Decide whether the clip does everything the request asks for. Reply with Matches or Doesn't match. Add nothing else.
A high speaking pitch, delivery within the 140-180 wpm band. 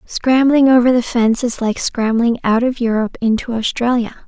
Matches